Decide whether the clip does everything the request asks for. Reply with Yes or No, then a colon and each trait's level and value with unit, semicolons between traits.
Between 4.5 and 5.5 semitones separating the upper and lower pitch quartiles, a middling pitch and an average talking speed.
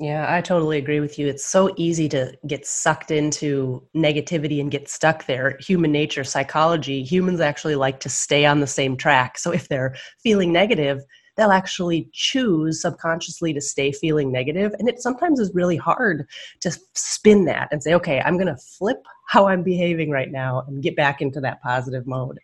No: average, 3.9 semitones; medium, 155 Hz; average, 190 wpm